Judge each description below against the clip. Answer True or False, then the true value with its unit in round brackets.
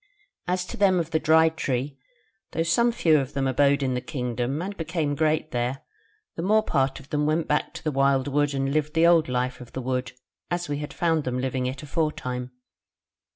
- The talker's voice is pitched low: False (145 Hz)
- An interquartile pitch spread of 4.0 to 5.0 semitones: False (3.6 semitones)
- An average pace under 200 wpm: False (205 wpm)